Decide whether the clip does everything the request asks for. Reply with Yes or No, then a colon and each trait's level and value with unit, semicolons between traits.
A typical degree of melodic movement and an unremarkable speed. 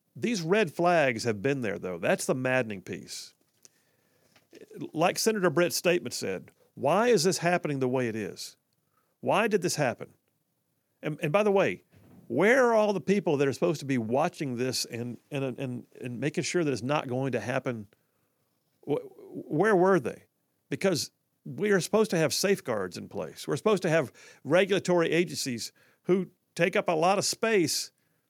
No: wide, 6.6 semitones; average, 175 wpm